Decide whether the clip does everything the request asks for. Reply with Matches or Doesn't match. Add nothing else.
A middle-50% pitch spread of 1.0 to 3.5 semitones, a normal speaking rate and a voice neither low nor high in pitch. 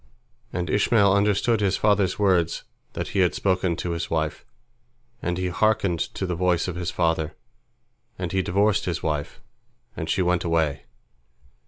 Doesn't match